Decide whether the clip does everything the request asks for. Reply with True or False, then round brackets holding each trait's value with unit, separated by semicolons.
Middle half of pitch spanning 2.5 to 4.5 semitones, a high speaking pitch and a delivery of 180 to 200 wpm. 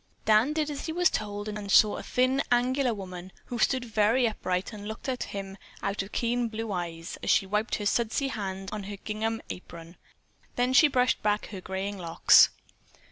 True (4.0 semitones; 215 Hz; 195 wpm)